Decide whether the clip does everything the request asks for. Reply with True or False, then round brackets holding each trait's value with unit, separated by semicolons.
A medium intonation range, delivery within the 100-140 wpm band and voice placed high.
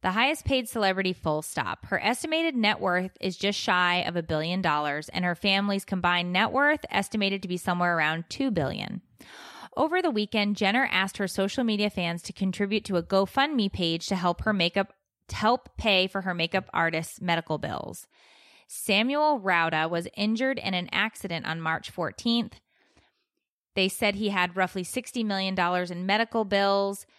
False (3.5 semitones; 170 wpm; 195 Hz)